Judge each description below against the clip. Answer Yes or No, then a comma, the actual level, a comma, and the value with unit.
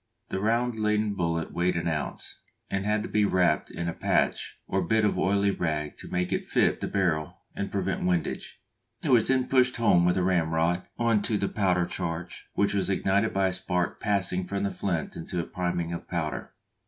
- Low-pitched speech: Yes, very low, 95 Hz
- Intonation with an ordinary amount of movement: Yes, average, 3.2 semitones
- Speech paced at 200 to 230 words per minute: Yes, fast, 205 wpm